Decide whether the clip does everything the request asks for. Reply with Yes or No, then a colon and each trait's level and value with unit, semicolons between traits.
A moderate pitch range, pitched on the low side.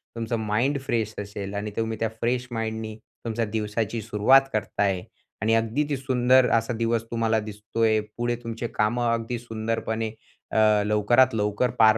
No: narrow, 1.7 semitones; low, 115 Hz